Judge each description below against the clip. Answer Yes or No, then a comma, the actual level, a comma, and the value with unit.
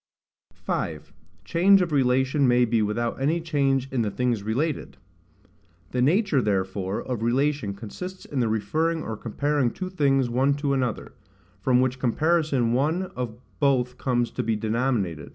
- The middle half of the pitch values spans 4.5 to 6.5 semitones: No, average, 4.1 semitones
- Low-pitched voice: Yes, low, 130 Hz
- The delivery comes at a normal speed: Yes, average, 155 wpm